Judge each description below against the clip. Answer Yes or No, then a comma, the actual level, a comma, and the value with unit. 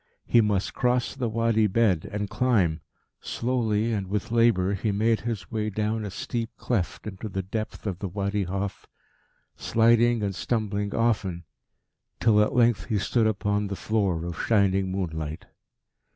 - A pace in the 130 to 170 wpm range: Yes, average, 155 wpm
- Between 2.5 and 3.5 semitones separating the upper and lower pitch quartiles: Yes, average, 2.9 semitones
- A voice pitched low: Yes, low, 105 Hz